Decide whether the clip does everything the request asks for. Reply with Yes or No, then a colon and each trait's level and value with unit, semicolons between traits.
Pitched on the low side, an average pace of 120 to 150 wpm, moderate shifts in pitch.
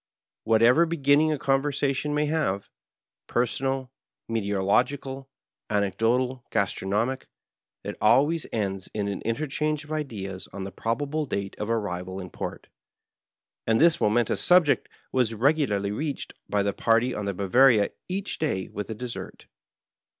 No: low, 120 Hz; average, 145 wpm; wide, 5.9 semitones